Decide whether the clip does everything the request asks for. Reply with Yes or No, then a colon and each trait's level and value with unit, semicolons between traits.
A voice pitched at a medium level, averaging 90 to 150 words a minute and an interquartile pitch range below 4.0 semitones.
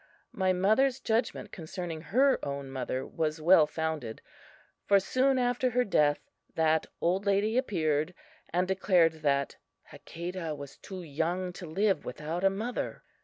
No: medium, 180 Hz; average, 140 wpm; average, 4.4 semitones